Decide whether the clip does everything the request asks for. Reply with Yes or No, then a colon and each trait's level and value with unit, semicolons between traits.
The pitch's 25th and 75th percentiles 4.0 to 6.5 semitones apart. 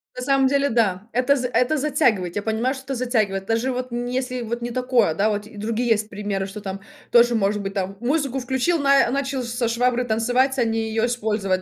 No: average, 3.3 semitones